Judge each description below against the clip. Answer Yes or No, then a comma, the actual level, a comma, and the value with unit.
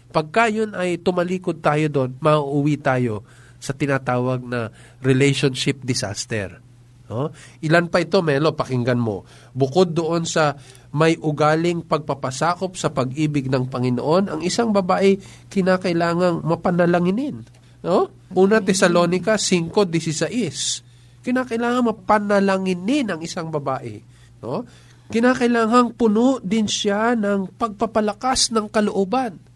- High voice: No, medium, 165 Hz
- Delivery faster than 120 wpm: No, slow, 110 wpm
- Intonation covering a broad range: Yes, wide, 7.2 semitones